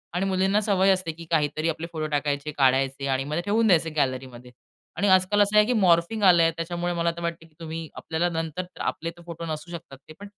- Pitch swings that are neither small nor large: Yes, average, 3.3 semitones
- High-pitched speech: No, medium, 165 Hz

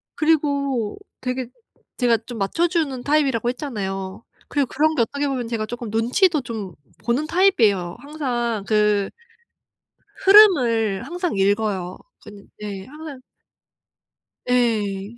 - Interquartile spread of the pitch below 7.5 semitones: Yes, wide, 5.5 semitones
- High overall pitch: Yes, high, 240 Hz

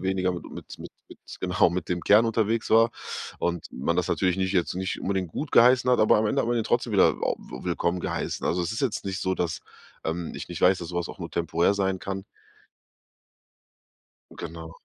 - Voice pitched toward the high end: No, very low, 95 Hz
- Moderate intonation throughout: Yes, average, 3.4 semitones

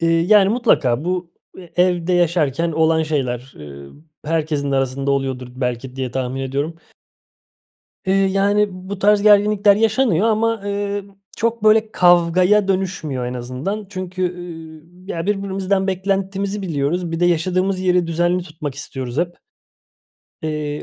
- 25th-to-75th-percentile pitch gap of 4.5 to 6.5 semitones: Yes, average, 5.0 semitones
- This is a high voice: No, medium, 175 Hz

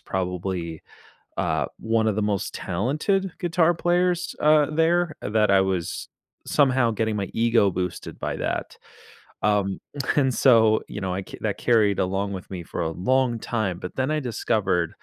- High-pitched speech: No, low, 110 Hz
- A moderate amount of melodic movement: No, wide, 6.2 semitones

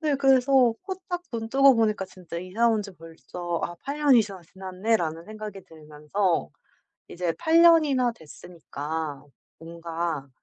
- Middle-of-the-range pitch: No, high, 195 Hz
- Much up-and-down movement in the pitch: Yes, wide, 7.4 semitones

